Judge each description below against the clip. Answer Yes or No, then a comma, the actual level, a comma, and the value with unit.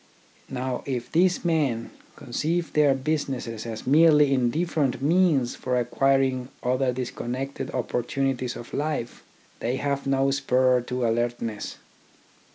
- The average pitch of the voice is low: Yes, low, 130 Hz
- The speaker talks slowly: Yes, slow, 120 wpm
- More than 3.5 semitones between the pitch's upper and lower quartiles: No, average, 2.7 semitones